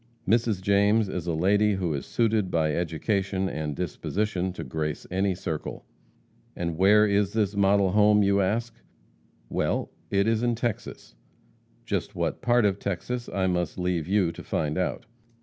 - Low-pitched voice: Yes, low, 100 Hz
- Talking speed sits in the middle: Yes, average, 160 wpm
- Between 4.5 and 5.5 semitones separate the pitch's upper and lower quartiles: No, average, 3.1 semitones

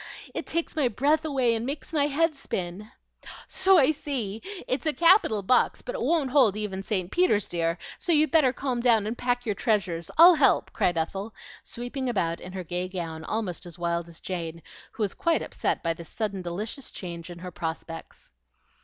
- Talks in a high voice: Yes, high, 215 Hz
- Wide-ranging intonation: Yes, wide, 7.9 semitones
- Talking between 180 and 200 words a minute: Yes, average, 195 wpm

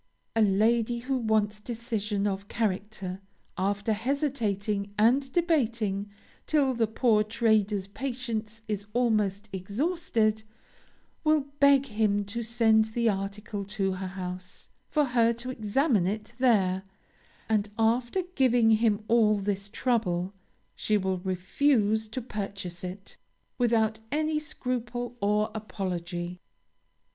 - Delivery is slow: Yes, slow, 115 wpm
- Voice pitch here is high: Yes, high, 215 Hz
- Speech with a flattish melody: No, average, 3.1 semitones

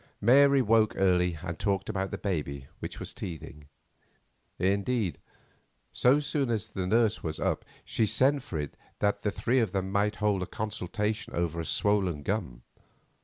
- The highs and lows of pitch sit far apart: No, average, 3.7 semitones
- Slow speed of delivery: No, average, 165 wpm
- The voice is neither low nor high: No, low, 100 Hz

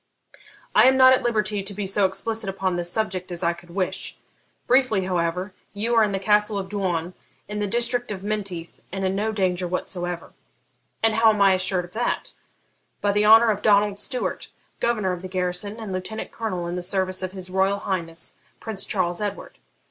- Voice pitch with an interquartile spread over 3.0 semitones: No, average, 2.7 semitones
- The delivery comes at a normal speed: Yes, average, 195 wpm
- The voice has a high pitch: Yes, high, 195 Hz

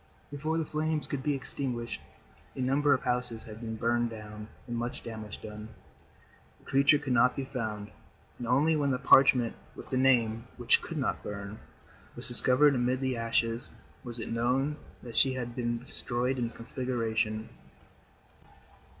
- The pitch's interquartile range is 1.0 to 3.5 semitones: Yes, average, 2.7 semitones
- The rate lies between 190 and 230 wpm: No, average, 165 wpm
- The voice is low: Yes, low, 125 Hz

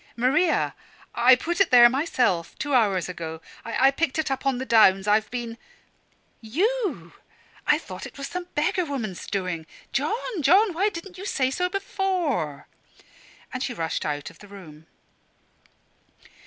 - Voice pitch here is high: Yes, very high, 260 Hz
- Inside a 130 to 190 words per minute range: Yes, average, 155 wpm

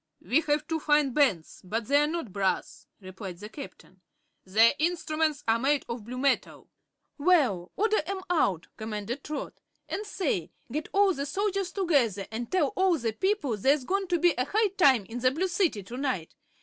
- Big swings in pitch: Yes, wide, 7.8 semitones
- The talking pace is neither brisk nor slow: Yes, average, 185 wpm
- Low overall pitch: No, very high, 280 Hz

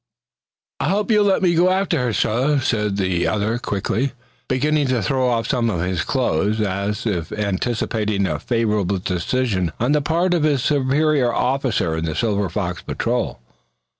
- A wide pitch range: Yes, wide, 5.8 semitones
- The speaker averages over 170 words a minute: No, average, 165 wpm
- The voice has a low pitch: Yes, low, 115 Hz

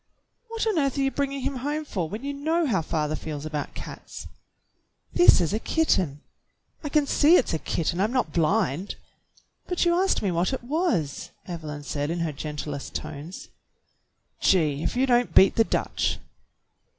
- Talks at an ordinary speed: Yes, average, 175 wpm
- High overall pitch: Yes, high, 205 Hz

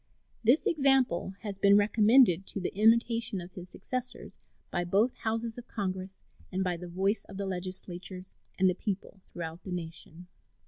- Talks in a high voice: Yes, high, 195 Hz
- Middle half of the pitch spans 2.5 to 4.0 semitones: Yes, average, 3.7 semitones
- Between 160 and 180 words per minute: Yes, average, 165 wpm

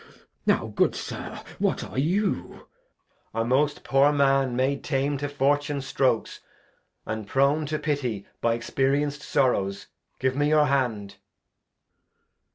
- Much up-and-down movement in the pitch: No, narrow, 2.4 semitones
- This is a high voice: No, low, 135 Hz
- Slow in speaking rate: Yes, slow, 130 wpm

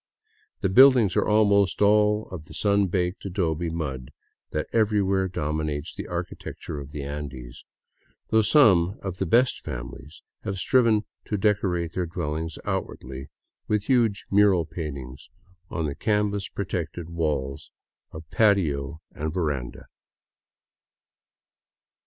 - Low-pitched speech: Yes, very low, 90 Hz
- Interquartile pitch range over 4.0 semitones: Yes, average, 5.2 semitones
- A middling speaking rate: No, slow, 130 wpm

